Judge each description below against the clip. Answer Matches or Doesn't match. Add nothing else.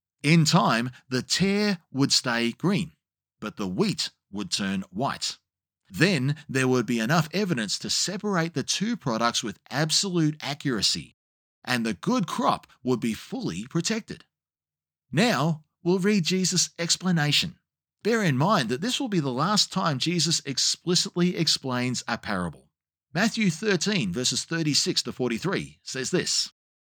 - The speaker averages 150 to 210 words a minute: Doesn't match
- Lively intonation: Matches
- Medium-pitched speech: Matches